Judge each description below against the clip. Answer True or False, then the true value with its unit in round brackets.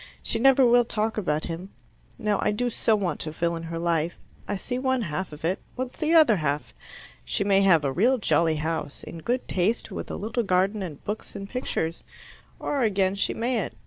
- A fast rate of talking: True (210 wpm)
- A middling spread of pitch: False (6.0 semitones)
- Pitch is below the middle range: False (195 Hz)